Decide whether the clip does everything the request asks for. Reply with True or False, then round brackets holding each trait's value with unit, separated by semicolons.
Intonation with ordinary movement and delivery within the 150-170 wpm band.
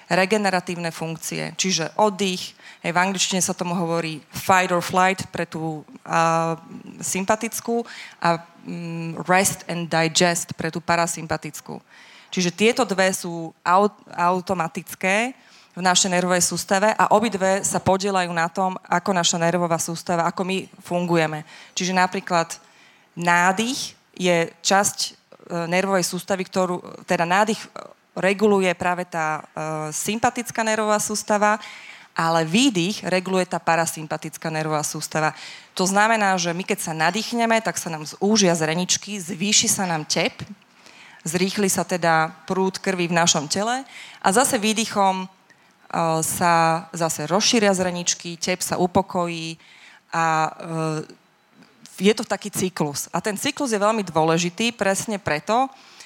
False (3.2 semitones; 130 wpm)